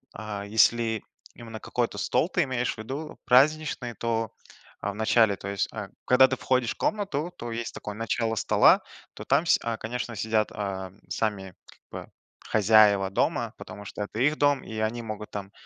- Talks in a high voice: No, low, 110 Hz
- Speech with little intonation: No, average, 3.0 semitones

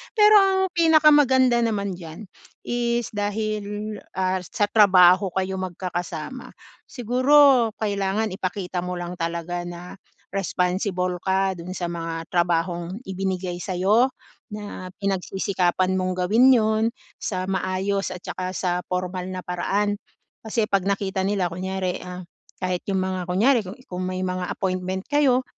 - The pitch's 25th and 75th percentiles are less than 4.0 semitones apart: Yes, average, 2.9 semitones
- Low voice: No, high, 190 Hz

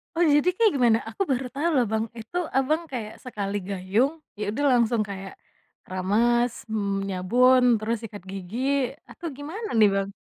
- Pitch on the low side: No, high, 225 Hz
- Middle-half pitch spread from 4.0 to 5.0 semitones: Yes, average, 4.6 semitones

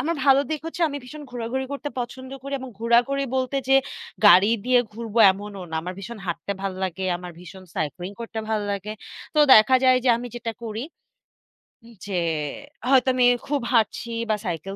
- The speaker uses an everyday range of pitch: Yes, average, 4.8 semitones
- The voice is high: Yes, high, 230 Hz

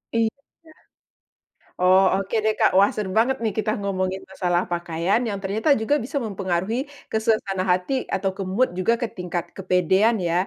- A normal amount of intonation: Yes, average, 3.1 semitones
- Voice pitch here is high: Yes, high, 195 Hz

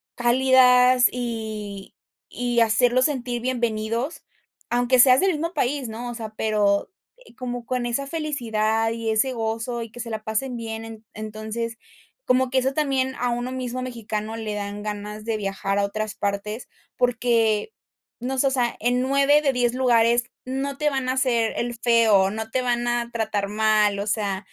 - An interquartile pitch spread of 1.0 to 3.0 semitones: Yes, average, 2.7 semitones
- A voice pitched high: Yes, high, 235 Hz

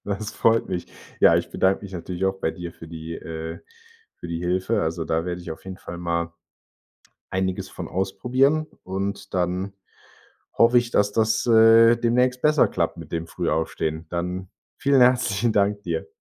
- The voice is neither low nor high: No, very low, 95 Hz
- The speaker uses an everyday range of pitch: Yes, average, 4.8 semitones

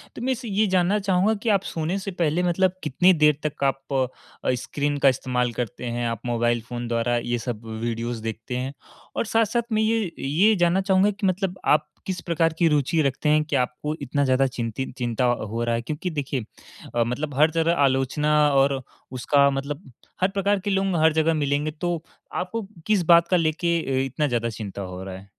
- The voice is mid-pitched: Yes, medium, 150 Hz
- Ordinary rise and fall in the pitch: No, wide, 6.5 semitones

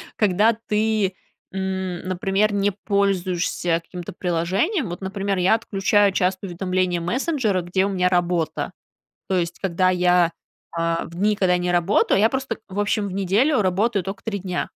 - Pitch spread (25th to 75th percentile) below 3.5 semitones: Yes, narrow, 2.5 semitones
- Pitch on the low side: No, high, 190 Hz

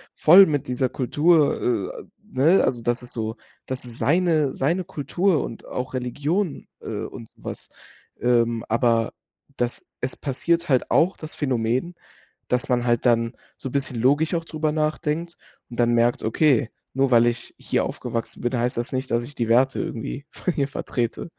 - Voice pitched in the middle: No, low, 130 Hz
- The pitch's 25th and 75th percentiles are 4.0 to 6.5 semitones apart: Yes, average, 4.4 semitones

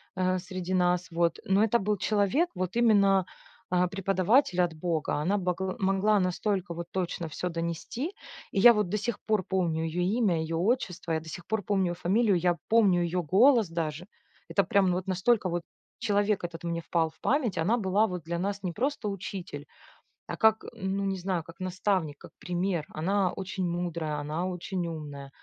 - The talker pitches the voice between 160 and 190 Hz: Yes, medium, 185 Hz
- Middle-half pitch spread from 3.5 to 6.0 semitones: No, average, 2.9 semitones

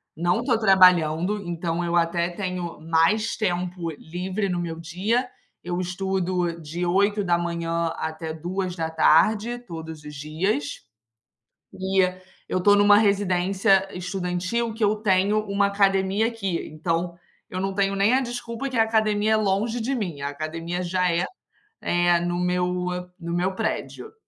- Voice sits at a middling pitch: Yes, medium, 180 Hz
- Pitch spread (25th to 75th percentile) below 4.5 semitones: Yes, average, 3.1 semitones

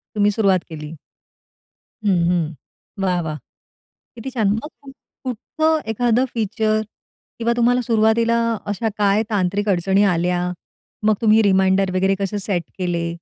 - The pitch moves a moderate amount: Yes, average, 3.4 semitones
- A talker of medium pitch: No, high, 205 Hz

